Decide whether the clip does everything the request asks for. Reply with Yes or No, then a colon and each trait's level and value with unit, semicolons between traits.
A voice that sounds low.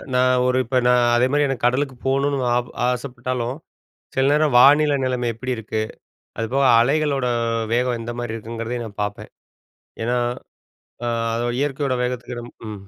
Yes: low, 125 Hz